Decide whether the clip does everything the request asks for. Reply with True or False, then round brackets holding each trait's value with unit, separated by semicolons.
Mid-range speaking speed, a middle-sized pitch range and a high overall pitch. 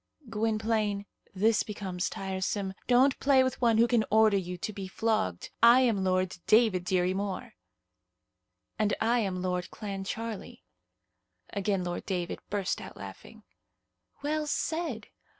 False (130 wpm; 3.3 semitones; 205 Hz)